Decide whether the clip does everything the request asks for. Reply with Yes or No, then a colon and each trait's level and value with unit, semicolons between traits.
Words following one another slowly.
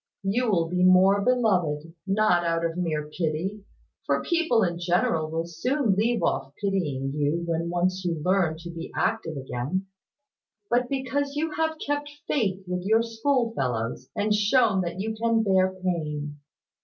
No: average, 155 wpm